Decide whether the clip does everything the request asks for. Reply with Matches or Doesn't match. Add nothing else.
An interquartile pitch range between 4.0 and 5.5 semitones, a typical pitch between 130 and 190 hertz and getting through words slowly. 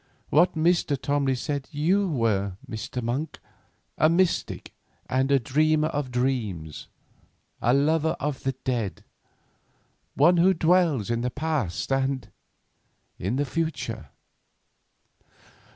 Matches